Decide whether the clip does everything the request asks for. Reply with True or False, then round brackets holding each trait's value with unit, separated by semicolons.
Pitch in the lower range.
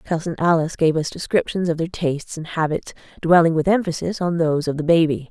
False (165 Hz)